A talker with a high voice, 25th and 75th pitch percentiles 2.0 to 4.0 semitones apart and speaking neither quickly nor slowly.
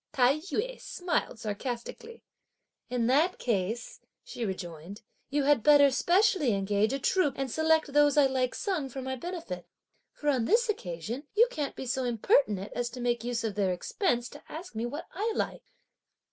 No: very high, 260 Hz; average, 5.3 semitones; average, 175 wpm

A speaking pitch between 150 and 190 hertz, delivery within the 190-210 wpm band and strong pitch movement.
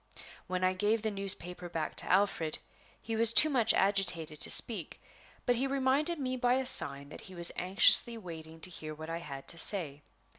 Yes: medium, 185 Hz; average, 195 wpm; wide, 5.9 semitones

